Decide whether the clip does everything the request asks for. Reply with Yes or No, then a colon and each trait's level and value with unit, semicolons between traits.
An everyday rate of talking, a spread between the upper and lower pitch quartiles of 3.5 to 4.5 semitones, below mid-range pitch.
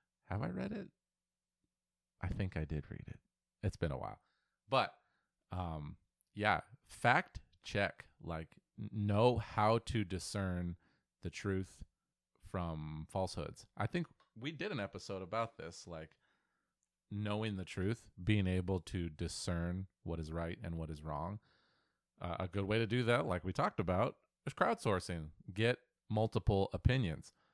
Yes: average, 145 wpm; average, 3.9 semitones; very low, 95 Hz